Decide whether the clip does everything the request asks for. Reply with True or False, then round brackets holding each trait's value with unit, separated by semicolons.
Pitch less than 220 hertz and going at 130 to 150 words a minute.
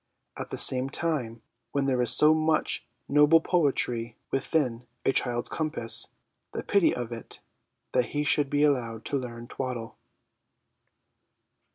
True (135 Hz; 140 wpm)